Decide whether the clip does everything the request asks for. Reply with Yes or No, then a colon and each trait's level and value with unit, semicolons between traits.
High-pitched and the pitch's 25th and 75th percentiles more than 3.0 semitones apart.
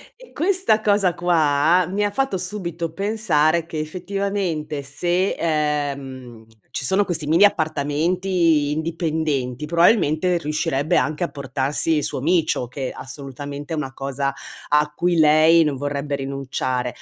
No: medium, 155 Hz; average, 3.8 semitones